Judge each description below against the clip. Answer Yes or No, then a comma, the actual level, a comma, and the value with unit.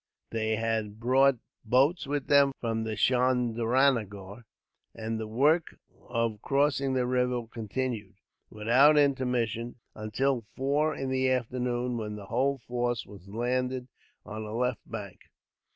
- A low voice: Yes, low, 125 Hz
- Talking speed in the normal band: No, slow, 125 wpm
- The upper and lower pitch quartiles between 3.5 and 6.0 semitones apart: No, average, 2.9 semitones